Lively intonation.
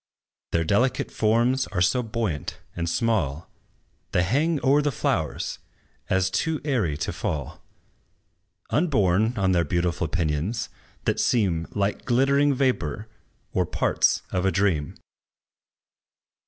Yes: wide, 6.6 semitones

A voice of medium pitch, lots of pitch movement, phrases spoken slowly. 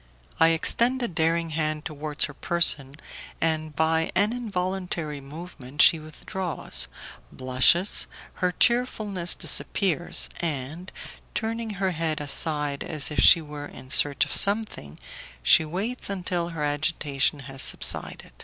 No: medium, 160 Hz; average, 3.8 semitones; slow, 125 wpm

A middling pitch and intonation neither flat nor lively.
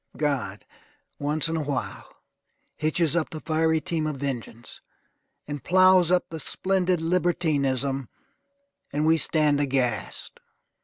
Yes: medium, 155 Hz; average, 3.1 semitones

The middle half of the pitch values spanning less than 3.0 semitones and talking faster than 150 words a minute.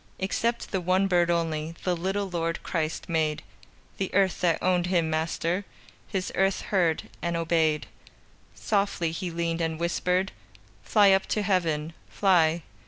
No: narrow, 2.6 semitones; average, 145 wpm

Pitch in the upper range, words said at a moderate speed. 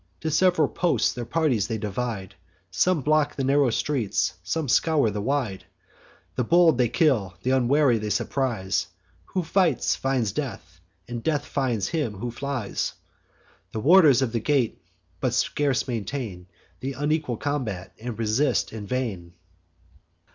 No: low, 125 Hz; average, 145 wpm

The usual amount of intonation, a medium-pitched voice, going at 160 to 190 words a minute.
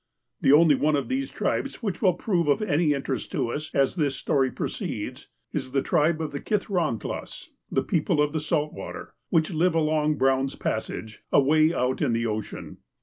Yes: average, 3.5 semitones; medium, 150 Hz; average, 185 wpm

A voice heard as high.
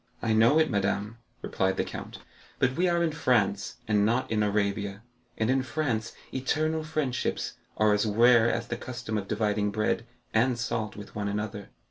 No: low, 110 Hz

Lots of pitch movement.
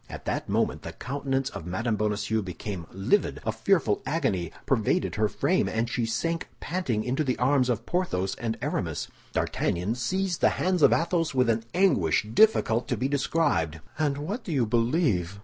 Yes: wide, 6.8 semitones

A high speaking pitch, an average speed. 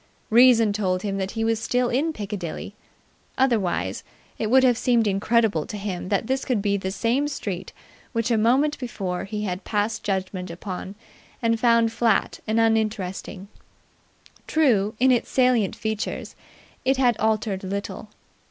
Yes: high, 220 Hz; average, 150 wpm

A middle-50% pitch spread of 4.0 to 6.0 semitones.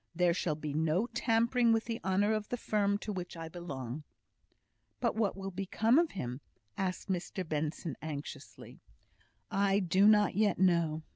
Yes: average, 4.8 semitones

